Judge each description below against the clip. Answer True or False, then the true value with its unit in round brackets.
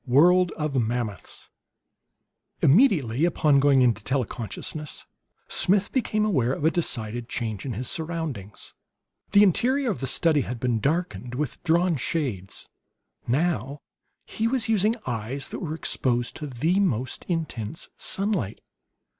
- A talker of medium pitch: True (145 Hz)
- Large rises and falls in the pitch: True (6.5 semitones)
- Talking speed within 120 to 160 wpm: True (140 wpm)